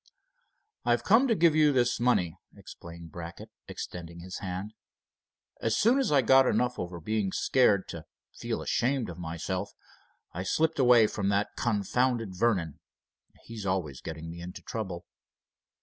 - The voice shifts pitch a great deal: Yes, wide, 6.1 semitones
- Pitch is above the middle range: No, low, 105 Hz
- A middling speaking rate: Yes, average, 150 wpm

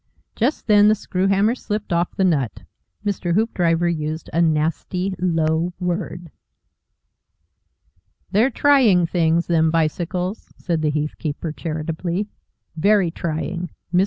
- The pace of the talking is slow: Yes, slow, 125 wpm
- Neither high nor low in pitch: Yes, medium, 175 Hz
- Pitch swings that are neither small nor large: Yes, average, 3.4 semitones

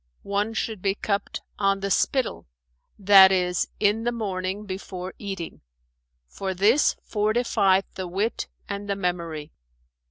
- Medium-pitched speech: No, high, 195 Hz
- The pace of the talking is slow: Yes, slow, 130 wpm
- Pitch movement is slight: Yes, narrow, 1.9 semitones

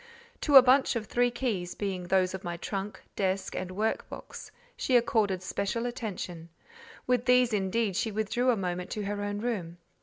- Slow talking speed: No, average, 180 wpm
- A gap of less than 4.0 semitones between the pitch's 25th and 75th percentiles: No, average, 4.3 semitones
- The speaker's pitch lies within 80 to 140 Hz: No, high, 205 Hz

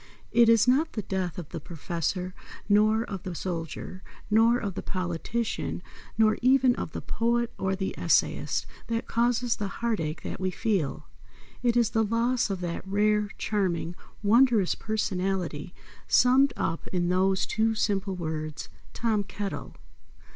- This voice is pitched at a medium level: No, high, 205 Hz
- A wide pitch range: No, average, 4.0 semitones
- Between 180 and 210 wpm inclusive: No, average, 150 wpm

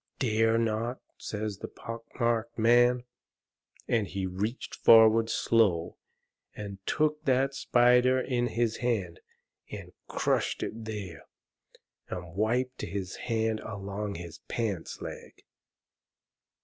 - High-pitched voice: No, low, 115 Hz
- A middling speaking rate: No, slow, 110 wpm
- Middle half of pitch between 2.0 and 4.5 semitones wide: Yes, average, 3.1 semitones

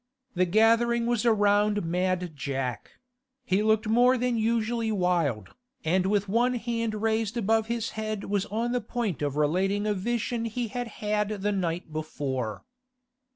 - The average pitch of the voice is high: Yes, high, 210 Hz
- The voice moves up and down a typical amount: Yes, average, 4.0 semitones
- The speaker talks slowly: No, average, 155 wpm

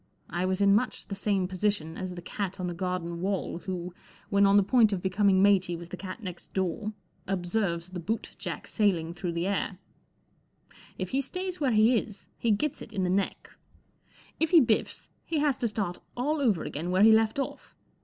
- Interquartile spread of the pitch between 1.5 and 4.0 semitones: Yes, average, 3.4 semitones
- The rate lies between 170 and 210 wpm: Yes, fast, 205 wpm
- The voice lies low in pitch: No, high, 195 Hz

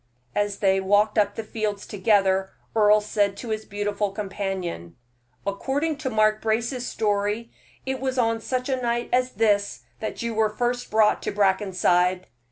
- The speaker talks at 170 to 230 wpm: No, average, 155 wpm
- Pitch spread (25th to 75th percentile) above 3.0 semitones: No, narrow, 2.4 semitones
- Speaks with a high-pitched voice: Yes, high, 210 Hz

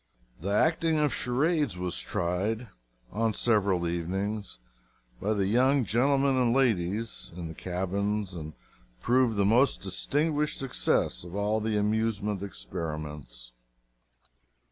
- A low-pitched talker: Yes, low, 105 Hz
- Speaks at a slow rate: Yes, slow, 120 wpm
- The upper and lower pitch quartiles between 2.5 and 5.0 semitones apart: No, wide, 5.5 semitones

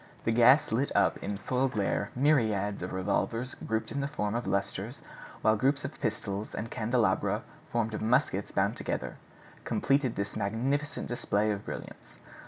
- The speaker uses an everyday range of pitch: Yes, average, 3.9 semitones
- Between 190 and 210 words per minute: No, average, 160 wpm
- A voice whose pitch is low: Yes, low, 115 Hz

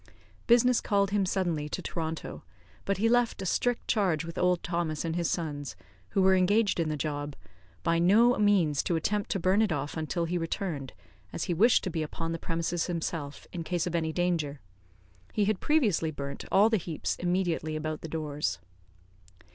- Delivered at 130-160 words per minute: No, average, 185 wpm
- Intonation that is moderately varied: Yes, average, 3.8 semitones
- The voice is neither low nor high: Yes, medium, 170 Hz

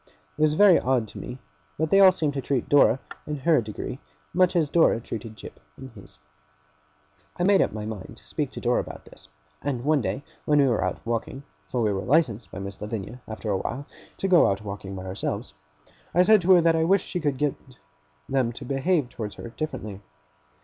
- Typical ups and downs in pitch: No, wide, 6.6 semitones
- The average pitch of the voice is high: No, low, 130 Hz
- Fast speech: Yes, fast, 215 wpm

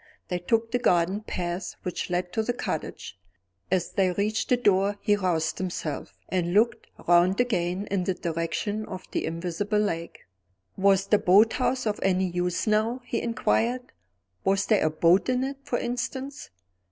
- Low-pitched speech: No, high, 195 Hz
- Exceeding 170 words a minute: No, average, 165 wpm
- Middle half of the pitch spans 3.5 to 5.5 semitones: Yes, average, 4.2 semitones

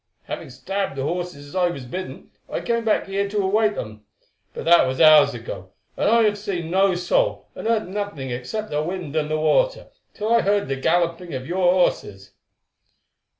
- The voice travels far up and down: Yes, wide, 6.1 semitones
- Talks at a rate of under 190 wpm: No, average, 195 wpm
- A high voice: No, medium, 180 Hz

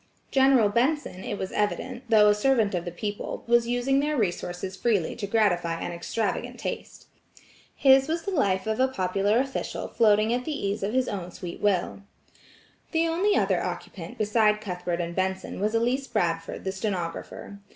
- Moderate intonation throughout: Yes, average, 5.0 semitones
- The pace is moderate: Yes, average, 170 wpm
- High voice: Yes, high, 210 Hz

